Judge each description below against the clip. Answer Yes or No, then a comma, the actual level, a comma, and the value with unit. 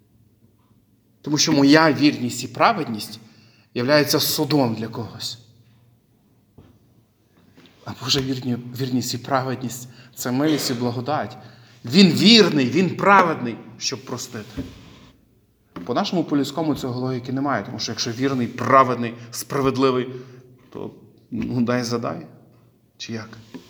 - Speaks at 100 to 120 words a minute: Yes, average, 110 wpm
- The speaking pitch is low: Yes, low, 125 Hz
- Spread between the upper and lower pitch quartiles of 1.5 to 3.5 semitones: Yes, average, 2.8 semitones